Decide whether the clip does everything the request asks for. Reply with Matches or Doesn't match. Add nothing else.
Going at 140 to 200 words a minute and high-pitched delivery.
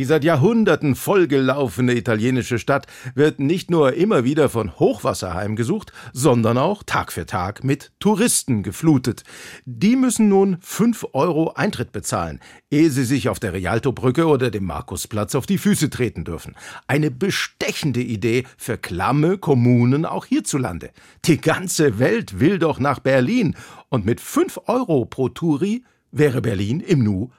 Doesn't match